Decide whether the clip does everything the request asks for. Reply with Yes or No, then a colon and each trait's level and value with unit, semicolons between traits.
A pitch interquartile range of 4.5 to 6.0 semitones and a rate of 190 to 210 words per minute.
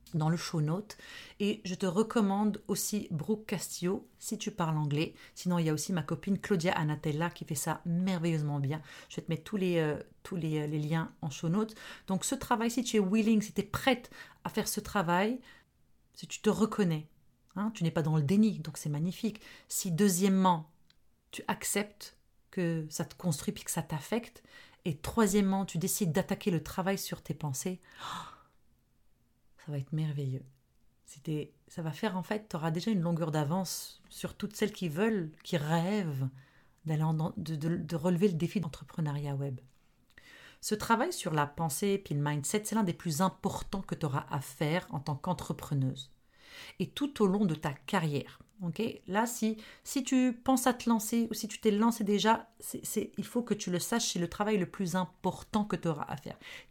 Yes: average, 4.9 semitones; average, 200 wpm